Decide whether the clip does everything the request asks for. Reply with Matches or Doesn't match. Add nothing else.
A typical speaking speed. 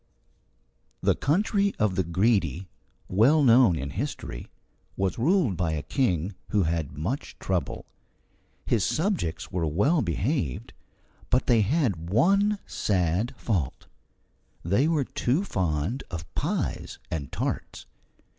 Doesn't match